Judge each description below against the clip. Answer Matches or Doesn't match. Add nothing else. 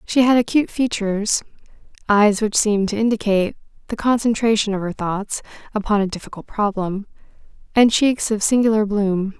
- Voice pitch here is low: Doesn't match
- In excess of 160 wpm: Doesn't match